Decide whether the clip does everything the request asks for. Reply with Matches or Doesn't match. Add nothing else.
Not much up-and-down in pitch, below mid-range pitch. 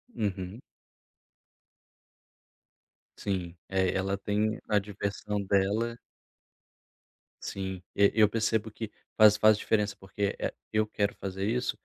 Matches